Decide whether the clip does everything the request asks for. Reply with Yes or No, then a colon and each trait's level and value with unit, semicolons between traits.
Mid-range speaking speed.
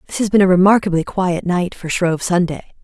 No: fast, 210 wpm